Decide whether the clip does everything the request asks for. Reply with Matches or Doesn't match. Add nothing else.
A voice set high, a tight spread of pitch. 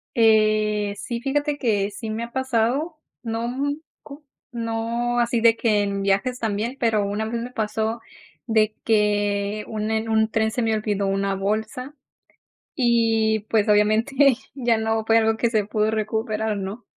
Matches